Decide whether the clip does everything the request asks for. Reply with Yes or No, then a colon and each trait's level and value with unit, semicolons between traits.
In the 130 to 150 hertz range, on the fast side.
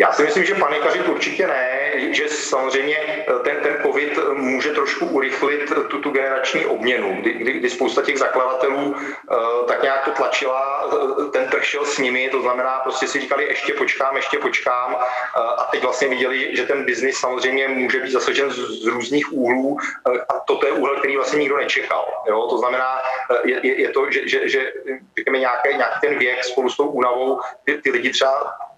Yes: medium, 140 Hz; fast, 185 wpm